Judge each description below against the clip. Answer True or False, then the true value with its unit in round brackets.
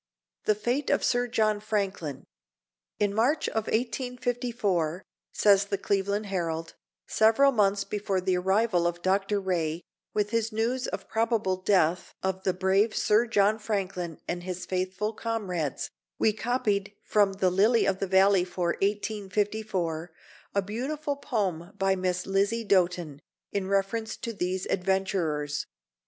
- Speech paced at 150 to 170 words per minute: False (140 wpm)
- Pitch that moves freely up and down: False (3.0 semitones)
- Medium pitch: False (200 Hz)